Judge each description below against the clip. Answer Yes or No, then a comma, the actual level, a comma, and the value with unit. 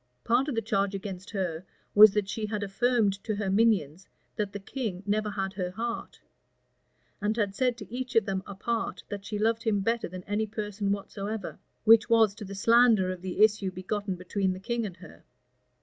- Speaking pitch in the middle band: No, high, 205 Hz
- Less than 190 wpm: No, average, 195 wpm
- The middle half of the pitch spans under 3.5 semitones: Yes, narrow, 2.6 semitones